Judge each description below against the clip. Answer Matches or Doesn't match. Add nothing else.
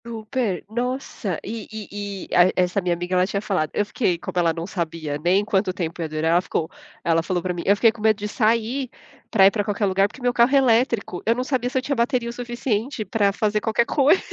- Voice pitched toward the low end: Doesn't match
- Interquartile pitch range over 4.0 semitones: Matches